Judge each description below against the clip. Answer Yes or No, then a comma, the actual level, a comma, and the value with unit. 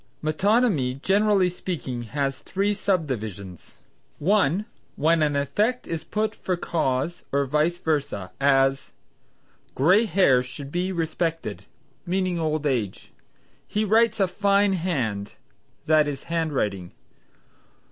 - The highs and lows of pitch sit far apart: Yes, wide, 5.8 semitones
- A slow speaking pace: Yes, slow, 115 wpm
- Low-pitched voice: No, medium, 160 Hz